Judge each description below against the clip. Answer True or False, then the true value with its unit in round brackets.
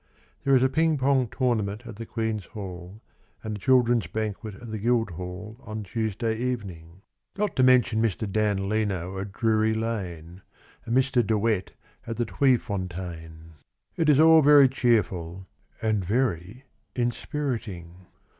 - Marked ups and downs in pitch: False (4.4 semitones)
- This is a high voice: False (110 Hz)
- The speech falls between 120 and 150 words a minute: True (145 wpm)